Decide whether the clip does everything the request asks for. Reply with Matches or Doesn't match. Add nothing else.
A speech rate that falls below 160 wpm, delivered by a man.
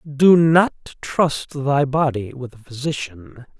Matches